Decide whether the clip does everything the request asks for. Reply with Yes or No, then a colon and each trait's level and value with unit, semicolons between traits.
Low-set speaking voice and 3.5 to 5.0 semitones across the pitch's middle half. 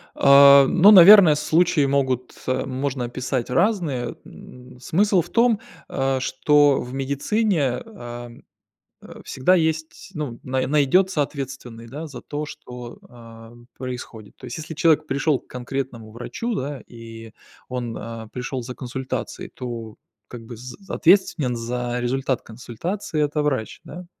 Yes: low, 130 Hz; average, 3.8 semitones